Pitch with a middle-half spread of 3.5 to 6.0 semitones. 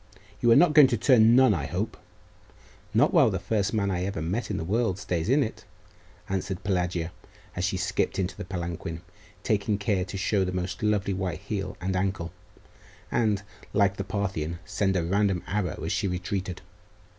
No: narrow, 2.6 semitones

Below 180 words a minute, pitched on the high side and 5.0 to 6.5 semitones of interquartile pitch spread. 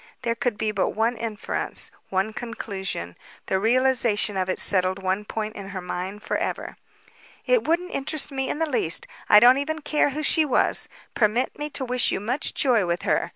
No: average, 190 wpm; high, 225 Hz; average, 5.3 semitones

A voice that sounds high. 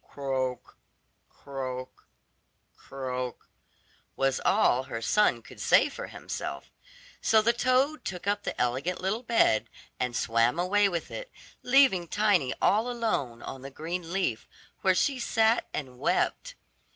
No: medium, 175 Hz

